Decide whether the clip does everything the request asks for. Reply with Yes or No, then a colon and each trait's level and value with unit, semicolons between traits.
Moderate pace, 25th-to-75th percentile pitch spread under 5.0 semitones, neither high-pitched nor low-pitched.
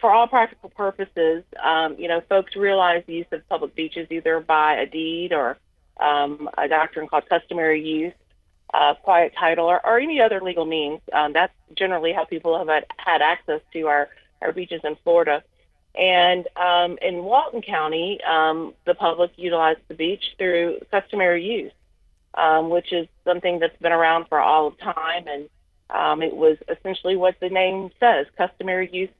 Yes: average, 175 wpm; narrow, 2.5 semitones; medium, 170 Hz